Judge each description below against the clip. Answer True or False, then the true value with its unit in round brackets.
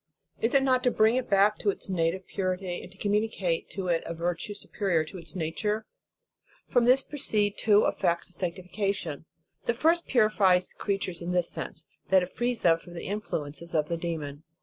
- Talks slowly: False (185 wpm)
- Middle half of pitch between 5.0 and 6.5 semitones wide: False (4.0 semitones)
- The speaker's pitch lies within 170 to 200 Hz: True (190 Hz)